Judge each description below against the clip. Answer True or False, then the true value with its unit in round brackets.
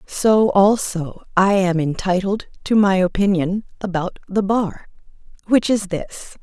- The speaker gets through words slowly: True (130 wpm)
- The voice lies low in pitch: False (195 Hz)